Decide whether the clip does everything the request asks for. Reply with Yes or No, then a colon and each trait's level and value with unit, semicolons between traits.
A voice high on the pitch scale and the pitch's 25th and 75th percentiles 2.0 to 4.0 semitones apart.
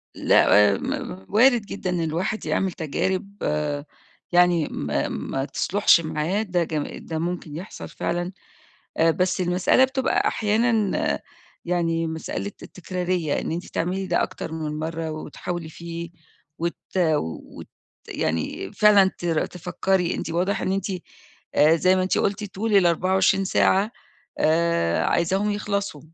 No: medium, 175 Hz; average, 3.0 semitones